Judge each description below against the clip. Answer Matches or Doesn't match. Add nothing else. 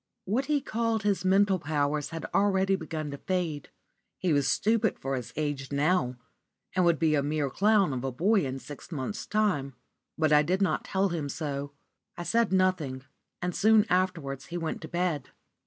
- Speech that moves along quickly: Doesn't match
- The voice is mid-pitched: Matches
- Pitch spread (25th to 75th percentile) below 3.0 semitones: Doesn't match